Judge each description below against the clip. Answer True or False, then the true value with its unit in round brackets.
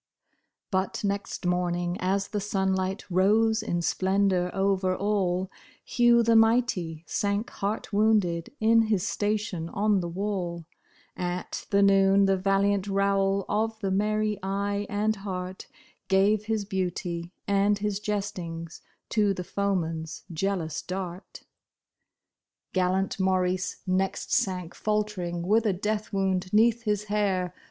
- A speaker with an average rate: False (125 wpm)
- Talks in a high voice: True (195 Hz)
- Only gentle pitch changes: True (2.2 semitones)